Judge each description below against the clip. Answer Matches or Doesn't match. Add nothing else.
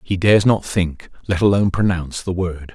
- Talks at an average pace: Matches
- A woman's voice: Doesn't match